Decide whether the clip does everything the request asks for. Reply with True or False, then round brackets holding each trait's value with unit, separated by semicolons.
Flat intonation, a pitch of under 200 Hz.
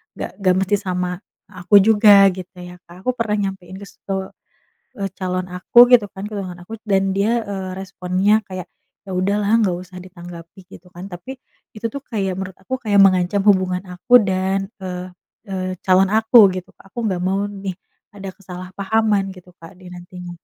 True (1.7 semitones; 190 Hz)